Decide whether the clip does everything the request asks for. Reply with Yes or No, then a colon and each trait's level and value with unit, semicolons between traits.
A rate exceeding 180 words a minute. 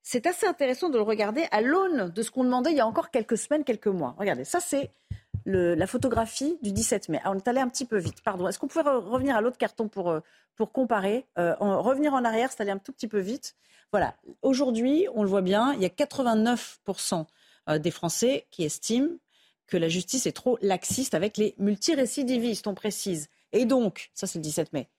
Yes: fast, 220 wpm